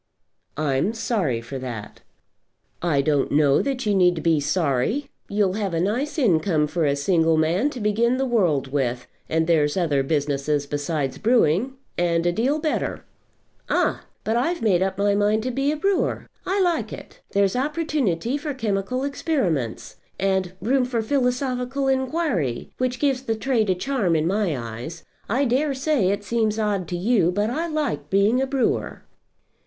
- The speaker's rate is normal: Yes, average, 170 wpm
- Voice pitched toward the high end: Yes, high, 205 Hz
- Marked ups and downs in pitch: Yes, wide, 8.1 semitones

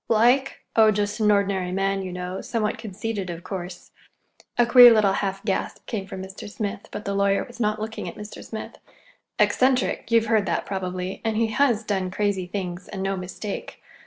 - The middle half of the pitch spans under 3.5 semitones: Yes, narrow, 2.5 semitones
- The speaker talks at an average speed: Yes, average, 180 wpm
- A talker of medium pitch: No, high, 205 Hz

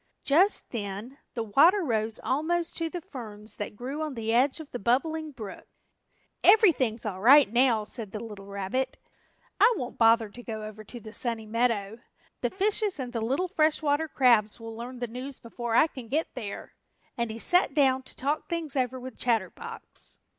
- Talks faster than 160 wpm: Yes, average, 185 wpm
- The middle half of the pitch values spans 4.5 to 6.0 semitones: Yes, average, 5.0 semitones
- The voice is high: Yes, very high, 250 Hz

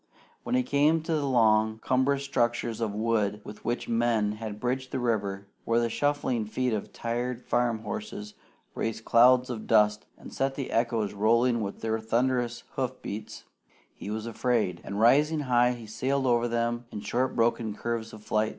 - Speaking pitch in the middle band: No, low, 115 Hz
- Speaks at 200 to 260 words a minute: No, average, 180 wpm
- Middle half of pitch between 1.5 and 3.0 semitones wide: Yes, narrow, 2.6 semitones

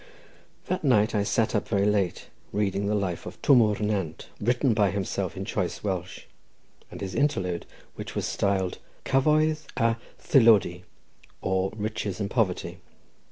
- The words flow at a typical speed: Yes, average, 150 wpm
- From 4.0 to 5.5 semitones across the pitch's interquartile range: No, average, 3.5 semitones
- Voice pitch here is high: No, low, 105 Hz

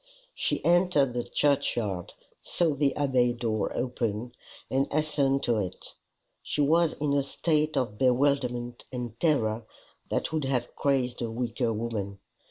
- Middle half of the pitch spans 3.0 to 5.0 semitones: Yes, average, 3.5 semitones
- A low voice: Yes, low, 125 Hz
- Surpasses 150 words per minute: No, average, 140 wpm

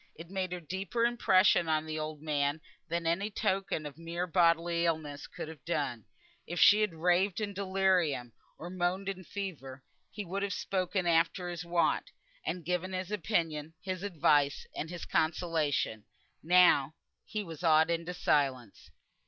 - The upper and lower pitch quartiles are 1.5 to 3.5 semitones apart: Yes, average, 3.1 semitones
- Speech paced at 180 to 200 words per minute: No, average, 160 wpm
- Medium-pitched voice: Yes, medium, 170 Hz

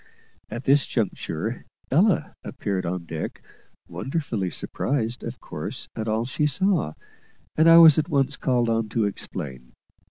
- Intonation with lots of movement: Yes, wide, 6.6 semitones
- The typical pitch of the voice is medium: No, low, 120 Hz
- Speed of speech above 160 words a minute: No, average, 140 wpm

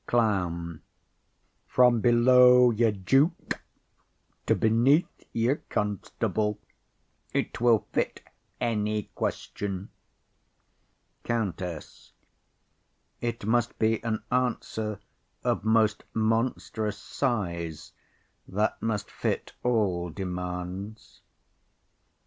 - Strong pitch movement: No, average, 3.3 semitones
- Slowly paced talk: Yes, slow, 80 wpm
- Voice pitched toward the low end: Yes, low, 110 Hz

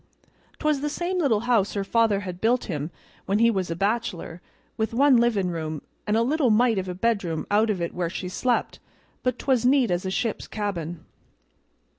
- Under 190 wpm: No, average, 195 wpm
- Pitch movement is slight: No, average, 4.8 semitones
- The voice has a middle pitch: No, high, 215 Hz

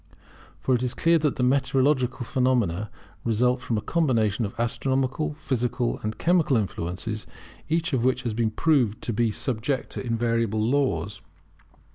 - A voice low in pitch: Yes, low, 125 Hz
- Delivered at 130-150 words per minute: Yes, average, 145 wpm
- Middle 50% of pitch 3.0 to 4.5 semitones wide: Yes, average, 3.3 semitones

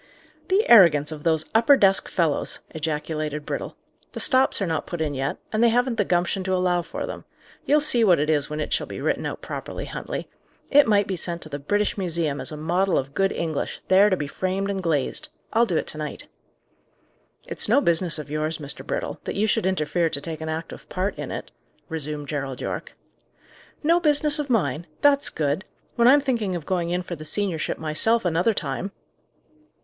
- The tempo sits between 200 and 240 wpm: Yes, fast, 205 wpm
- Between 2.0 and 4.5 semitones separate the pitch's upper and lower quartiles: No, average, 5.2 semitones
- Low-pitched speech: No, medium, 175 Hz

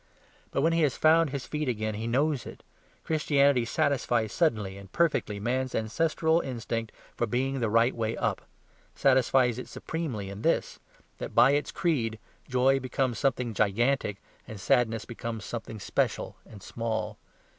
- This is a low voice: Yes, low, 125 Hz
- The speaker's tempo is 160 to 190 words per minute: No, average, 150 wpm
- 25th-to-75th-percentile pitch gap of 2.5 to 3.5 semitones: No, average, 4.0 semitones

